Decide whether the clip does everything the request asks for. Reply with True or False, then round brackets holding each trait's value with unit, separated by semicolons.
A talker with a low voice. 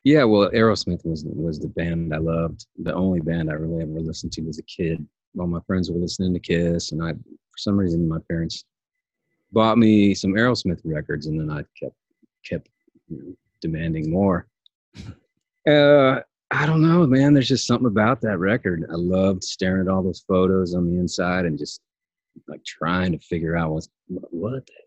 True (90 Hz)